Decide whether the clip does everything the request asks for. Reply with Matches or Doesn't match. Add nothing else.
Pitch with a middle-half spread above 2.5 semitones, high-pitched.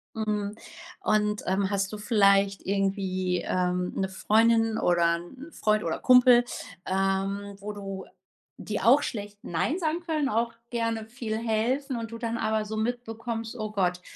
Matches